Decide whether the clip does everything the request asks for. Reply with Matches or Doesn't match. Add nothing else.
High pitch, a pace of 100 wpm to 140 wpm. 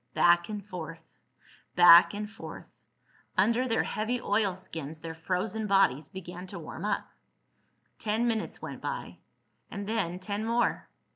Matches